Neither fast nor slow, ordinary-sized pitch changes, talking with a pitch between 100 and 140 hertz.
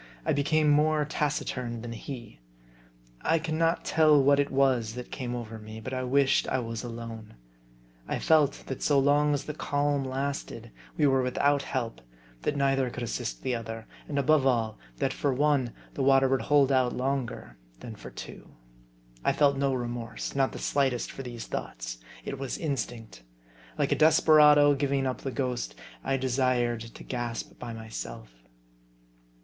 Yes: average, 170 wpm; average, 3.1 semitones; low, 135 Hz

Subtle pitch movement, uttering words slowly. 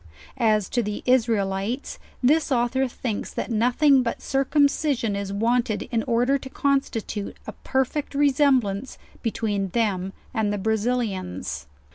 No: average, 4.3 semitones; slow, 130 wpm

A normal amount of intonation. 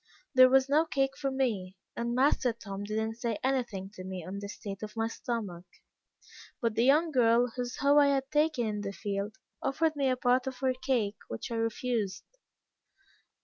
Yes: average, 4.4 semitones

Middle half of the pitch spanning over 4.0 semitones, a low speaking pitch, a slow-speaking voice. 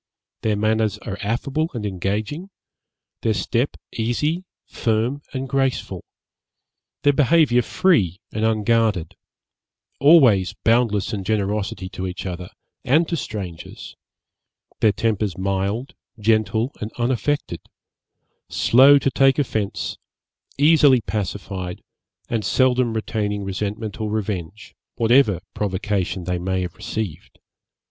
Yes: average, 4.5 semitones; low, 110 Hz; slow, 110 wpm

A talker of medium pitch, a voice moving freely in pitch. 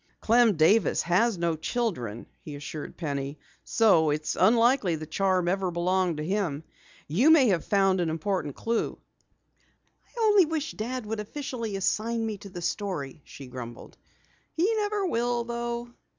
No: high, 200 Hz; wide, 6.6 semitones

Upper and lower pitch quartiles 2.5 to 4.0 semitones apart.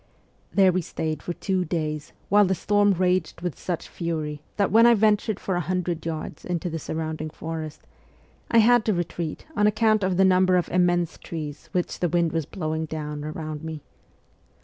Yes: average, 3.2 semitones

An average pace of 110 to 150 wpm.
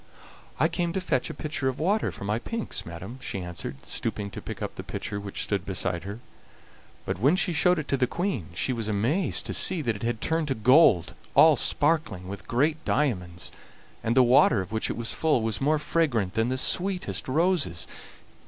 No: fast, 205 wpm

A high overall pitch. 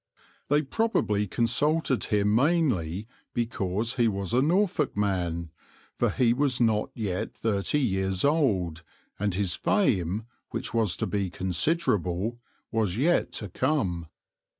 No: low, 110 Hz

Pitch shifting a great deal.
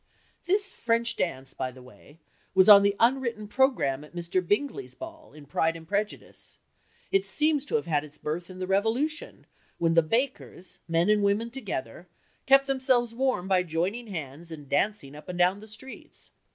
Yes: wide, 7.1 semitones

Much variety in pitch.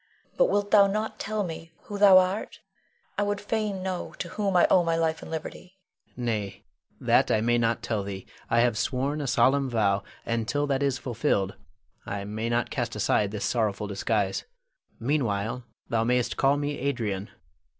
Yes: wide, 7.8 semitones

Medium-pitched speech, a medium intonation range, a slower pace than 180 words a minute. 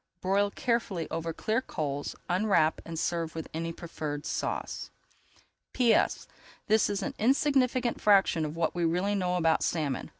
Yes: medium, 175 Hz; average, 4.7 semitones; average, 145 wpm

